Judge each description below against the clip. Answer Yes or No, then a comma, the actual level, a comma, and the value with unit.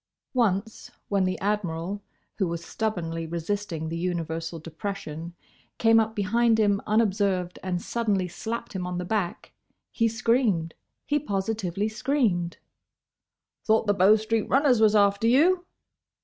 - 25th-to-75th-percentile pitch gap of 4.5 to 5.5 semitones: No, average, 4.1 semitones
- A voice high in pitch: Yes, high, 200 Hz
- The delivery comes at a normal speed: No, slow, 130 wpm